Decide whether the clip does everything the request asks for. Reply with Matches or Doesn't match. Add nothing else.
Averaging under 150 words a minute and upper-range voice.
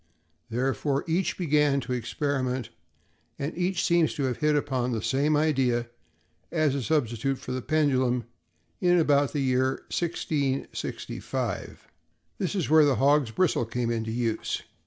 Doesn't match